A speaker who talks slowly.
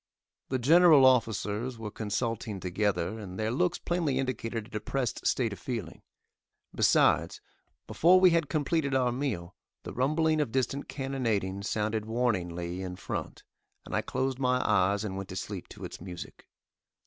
No: average, 155 wpm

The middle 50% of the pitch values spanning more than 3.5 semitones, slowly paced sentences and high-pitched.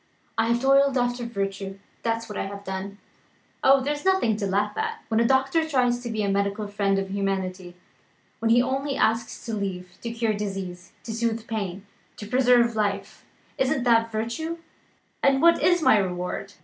No: average, 4.0 semitones; average, 175 wpm; high, 225 Hz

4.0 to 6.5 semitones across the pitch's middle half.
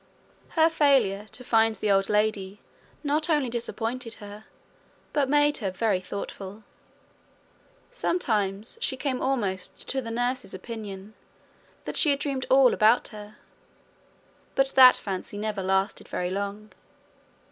Yes: average, 4.8 semitones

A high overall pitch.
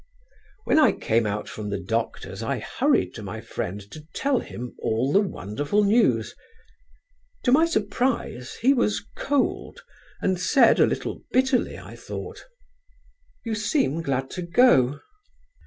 No: medium, 180 Hz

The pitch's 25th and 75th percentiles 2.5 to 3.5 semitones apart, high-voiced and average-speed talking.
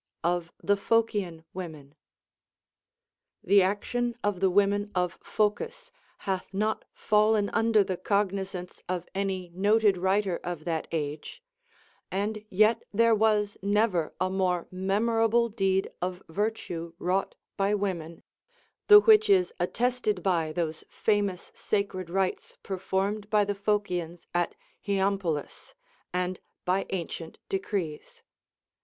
No: average, 2.9 semitones; high, 195 Hz; slow, 125 wpm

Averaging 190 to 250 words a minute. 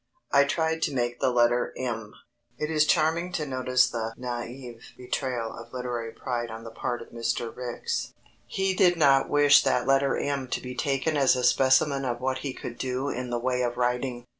Yes: average, 195 wpm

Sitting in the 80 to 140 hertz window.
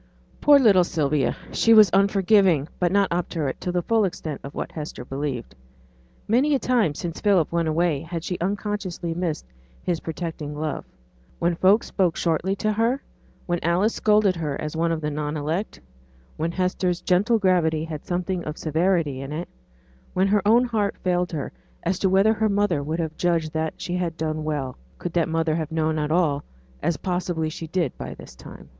No: medium, 170 Hz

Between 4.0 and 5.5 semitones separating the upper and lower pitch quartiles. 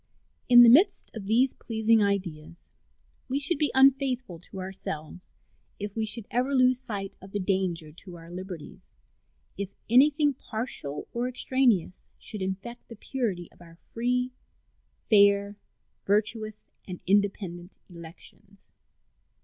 Yes: average, 5.2 semitones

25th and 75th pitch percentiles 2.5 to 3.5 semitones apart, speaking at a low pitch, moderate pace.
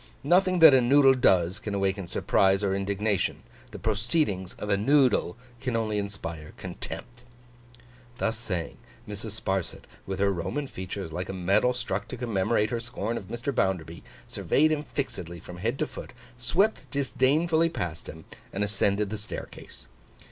No: average, 4.6 semitones; low, 105 Hz; average, 155 wpm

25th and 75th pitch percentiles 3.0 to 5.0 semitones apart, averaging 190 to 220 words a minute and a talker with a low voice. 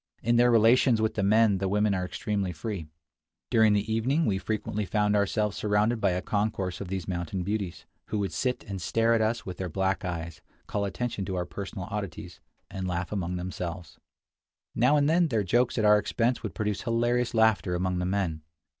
Yes: average, 3.3 semitones; average, 200 wpm; low, 105 Hz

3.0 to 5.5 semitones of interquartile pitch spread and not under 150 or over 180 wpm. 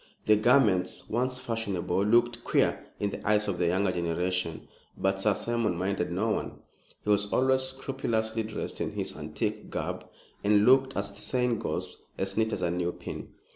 Yes: average, 3.8 semitones; average, 175 wpm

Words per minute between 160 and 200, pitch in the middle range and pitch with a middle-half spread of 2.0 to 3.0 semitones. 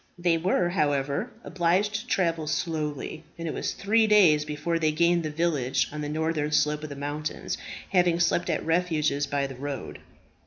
Yes: average, 180 wpm; medium, 160 Hz; average, 2.7 semitones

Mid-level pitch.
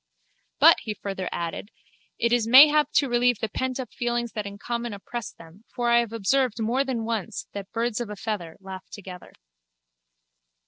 No: high, 230 Hz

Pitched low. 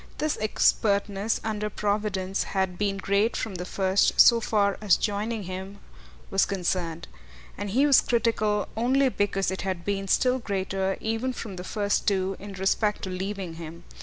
No: high, 200 Hz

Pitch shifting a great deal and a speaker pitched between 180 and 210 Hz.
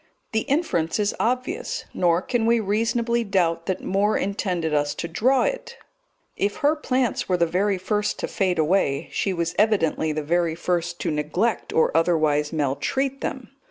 Yes: wide, 5.7 semitones; medium, 185 Hz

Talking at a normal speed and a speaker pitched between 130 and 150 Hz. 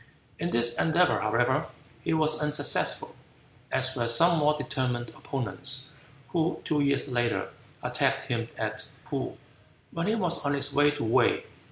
Yes: average, 150 wpm; medium, 140 Hz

